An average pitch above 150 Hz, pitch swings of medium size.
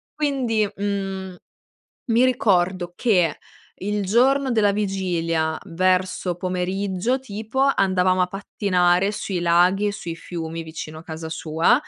Yes: medium, 185 Hz; average, 3.0 semitones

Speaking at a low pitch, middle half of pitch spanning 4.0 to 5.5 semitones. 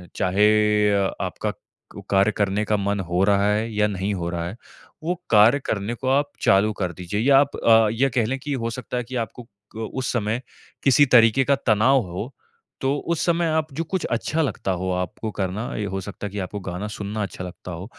Yes: low, 105 Hz; average, 4.6 semitones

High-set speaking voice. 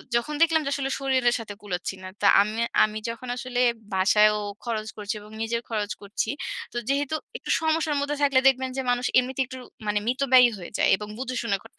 Yes: high, 245 Hz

